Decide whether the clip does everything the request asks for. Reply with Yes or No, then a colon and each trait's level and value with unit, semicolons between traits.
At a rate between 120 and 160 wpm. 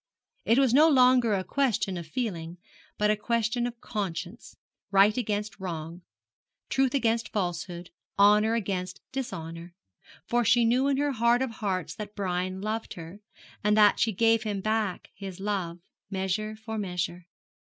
Yes: average, 155 wpm